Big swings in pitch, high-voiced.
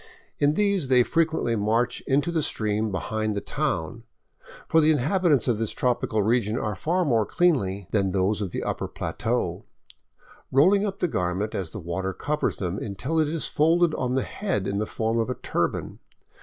No: wide, 7.4 semitones; low, 115 Hz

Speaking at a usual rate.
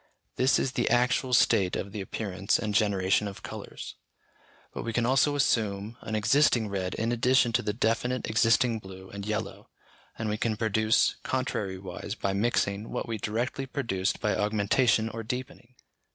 Yes: average, 165 wpm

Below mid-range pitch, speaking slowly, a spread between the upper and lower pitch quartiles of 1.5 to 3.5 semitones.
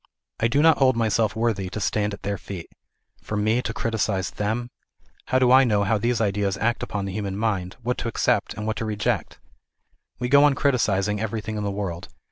No: low, 110 Hz; fast, 205 wpm; average, 2.7 semitones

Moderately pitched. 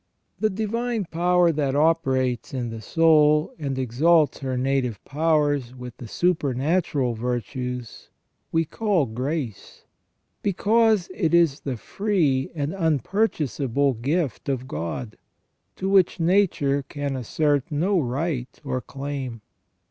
Yes: medium, 145 Hz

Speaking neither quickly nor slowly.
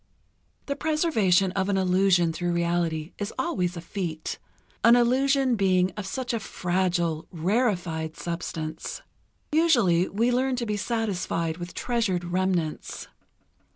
No: slow, 125 wpm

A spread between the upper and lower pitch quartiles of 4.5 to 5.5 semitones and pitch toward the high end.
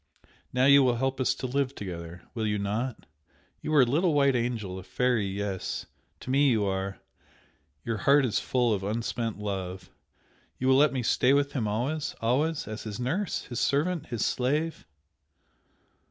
No: average, 5.0 semitones; low, 125 Hz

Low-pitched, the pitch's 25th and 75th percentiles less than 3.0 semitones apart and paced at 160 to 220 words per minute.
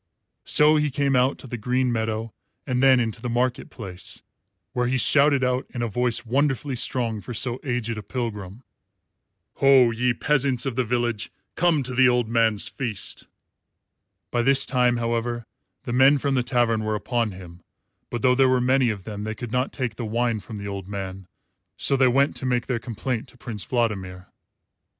Yes: low, 120 Hz; narrow, 2.6 semitones; average, 190 wpm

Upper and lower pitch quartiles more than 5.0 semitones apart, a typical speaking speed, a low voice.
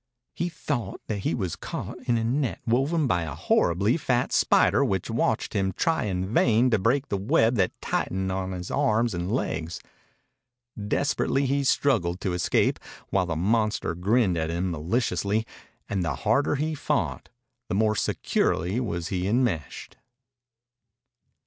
Yes: wide, 5.5 semitones; average, 155 wpm; low, 105 Hz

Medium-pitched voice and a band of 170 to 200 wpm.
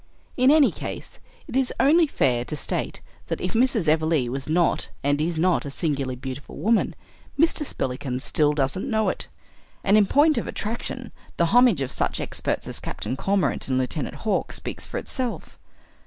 Yes: medium, 170 Hz; average, 175 wpm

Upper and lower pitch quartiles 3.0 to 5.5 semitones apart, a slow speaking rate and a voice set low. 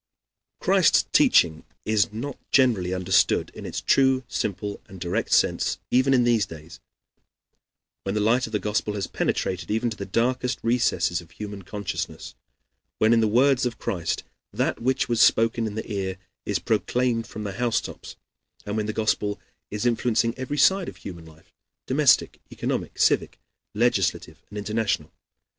No: average, 3.5 semitones; average, 160 wpm; low, 110 Hz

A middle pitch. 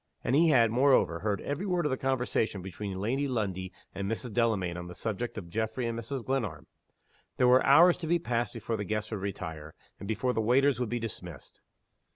No: low, 115 Hz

